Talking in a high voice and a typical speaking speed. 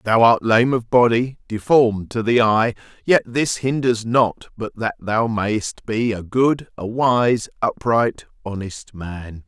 No: low, 115 Hz; average, 160 wpm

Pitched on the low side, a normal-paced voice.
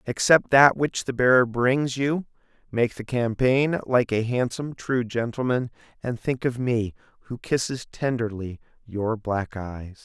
Yes: low, 120 Hz; average, 150 wpm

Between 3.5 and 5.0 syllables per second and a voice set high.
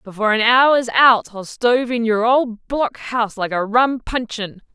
Yes: 4.5 syllables/s; high, 230 Hz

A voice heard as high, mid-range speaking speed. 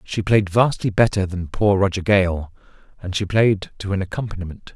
No: very low, 95 Hz; average, 175 wpm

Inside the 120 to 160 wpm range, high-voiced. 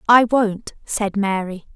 Yes: slow, 135 wpm; high, 210 Hz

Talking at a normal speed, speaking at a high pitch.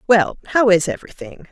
Yes: average, 160 wpm; high, 200 Hz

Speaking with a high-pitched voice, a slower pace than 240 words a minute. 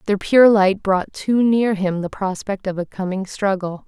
Yes: high, 195 Hz; average, 200 wpm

